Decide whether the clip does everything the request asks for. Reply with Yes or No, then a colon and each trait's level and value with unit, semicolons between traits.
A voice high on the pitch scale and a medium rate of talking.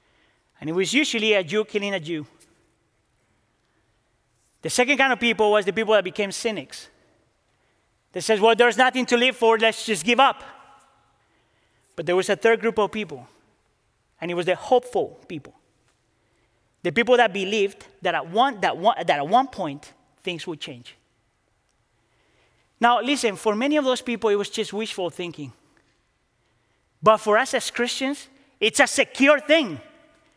Yes: high, 205 Hz; average, 165 wpm